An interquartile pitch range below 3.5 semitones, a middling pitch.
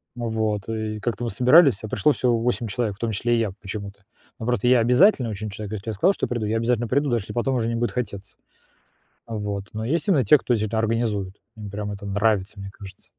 No: average, 2.8 semitones; low, 110 Hz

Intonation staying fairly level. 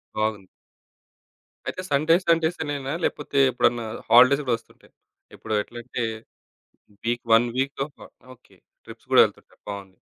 No: average, 3.7 semitones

